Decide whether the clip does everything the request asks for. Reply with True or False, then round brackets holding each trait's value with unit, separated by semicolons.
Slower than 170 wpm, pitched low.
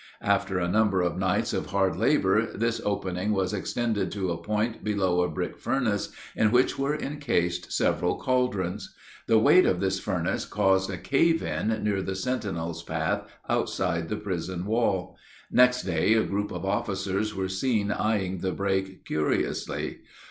True (160 wpm; 100 Hz)